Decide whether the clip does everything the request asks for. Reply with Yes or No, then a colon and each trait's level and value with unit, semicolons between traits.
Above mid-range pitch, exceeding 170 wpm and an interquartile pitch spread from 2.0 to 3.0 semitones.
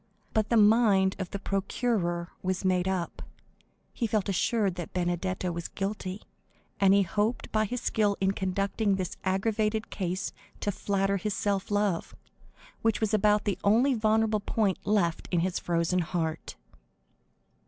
No: high, 195 Hz; average, 150 wpm; narrow, 2.6 semitones